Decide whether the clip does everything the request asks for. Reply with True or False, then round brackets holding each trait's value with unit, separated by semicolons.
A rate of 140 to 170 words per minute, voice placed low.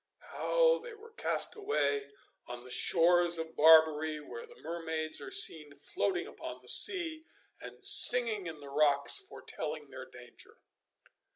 False (145 wpm; 170 Hz)